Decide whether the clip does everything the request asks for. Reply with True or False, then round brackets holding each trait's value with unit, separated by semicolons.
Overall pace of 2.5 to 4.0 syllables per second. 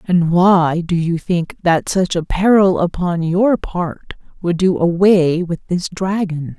True (3.7 syllables/s)